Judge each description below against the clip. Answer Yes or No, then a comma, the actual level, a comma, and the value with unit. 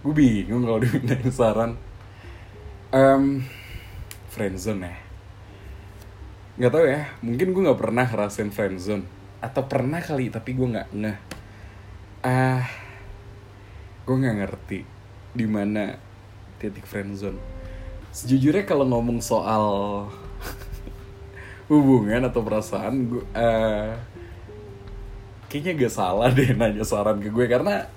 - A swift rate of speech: No, average, 115 wpm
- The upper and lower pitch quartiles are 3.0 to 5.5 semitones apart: Yes, average, 3.7 semitones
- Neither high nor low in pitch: No, low, 105 Hz